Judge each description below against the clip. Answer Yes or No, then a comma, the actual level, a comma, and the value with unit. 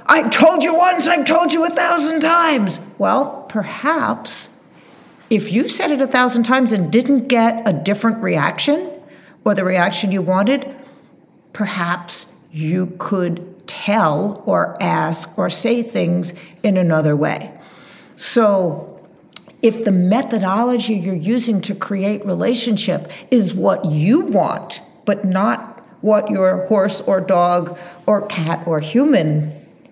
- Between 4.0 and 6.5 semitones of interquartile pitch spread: Yes, wide, 5.4 semitones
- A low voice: No, high, 210 Hz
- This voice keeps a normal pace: No, slow, 130 wpm